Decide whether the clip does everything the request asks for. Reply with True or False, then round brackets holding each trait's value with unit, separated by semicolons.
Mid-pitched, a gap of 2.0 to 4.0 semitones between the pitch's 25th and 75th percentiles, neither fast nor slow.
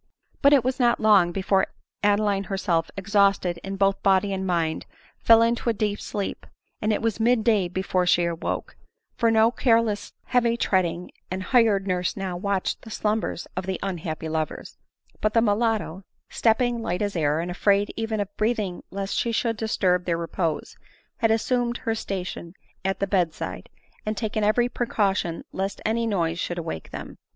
False (200 Hz; 3.7 semitones; 175 wpm)